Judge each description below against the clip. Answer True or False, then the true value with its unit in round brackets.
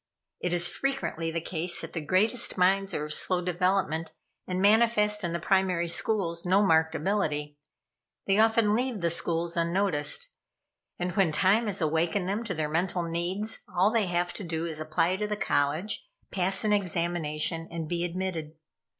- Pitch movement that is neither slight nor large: True (3.3 semitones)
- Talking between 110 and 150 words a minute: False (175 wpm)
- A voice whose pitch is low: False (180 Hz)